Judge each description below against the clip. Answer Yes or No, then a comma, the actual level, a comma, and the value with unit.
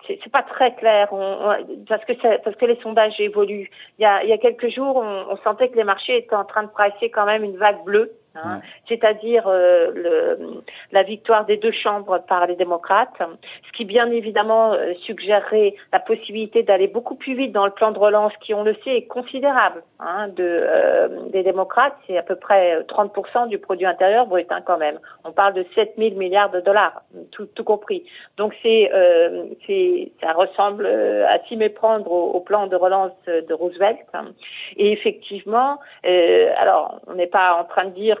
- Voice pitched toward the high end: Yes, high, 210 Hz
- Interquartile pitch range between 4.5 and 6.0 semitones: No, average, 3.4 semitones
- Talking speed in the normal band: Yes, average, 200 wpm